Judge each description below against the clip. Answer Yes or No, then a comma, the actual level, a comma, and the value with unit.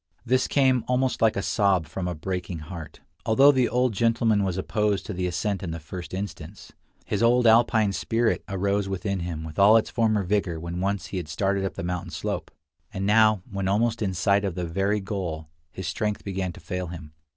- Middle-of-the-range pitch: No, low, 100 Hz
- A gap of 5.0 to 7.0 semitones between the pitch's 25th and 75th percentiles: No, average, 3.4 semitones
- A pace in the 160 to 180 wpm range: No, fast, 205 wpm